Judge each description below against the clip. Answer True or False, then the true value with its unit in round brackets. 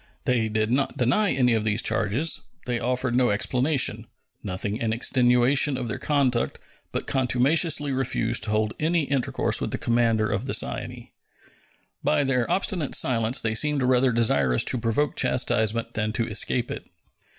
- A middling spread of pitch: True (3.2 semitones)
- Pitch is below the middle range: True (125 Hz)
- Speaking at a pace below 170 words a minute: True (160 wpm)